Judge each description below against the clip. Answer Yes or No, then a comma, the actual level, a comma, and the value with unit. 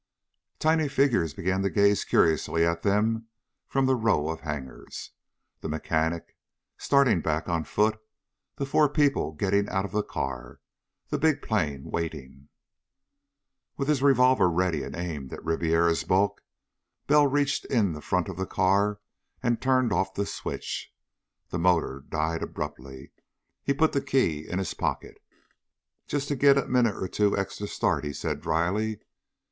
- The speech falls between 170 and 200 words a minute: No, average, 155 wpm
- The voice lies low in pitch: Yes, very low, 95 Hz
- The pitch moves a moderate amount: No, wide, 7.6 semitones